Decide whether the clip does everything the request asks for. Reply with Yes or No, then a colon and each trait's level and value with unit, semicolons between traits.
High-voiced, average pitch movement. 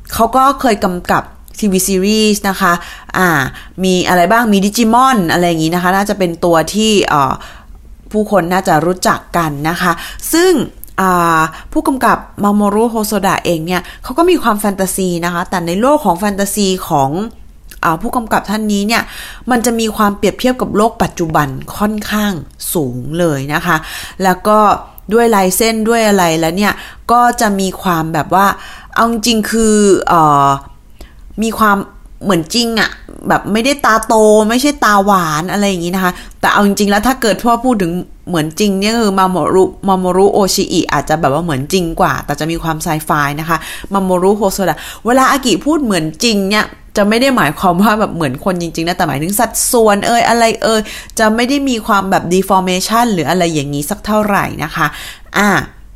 Yes: high, 195 Hz; average, 4.2 semitones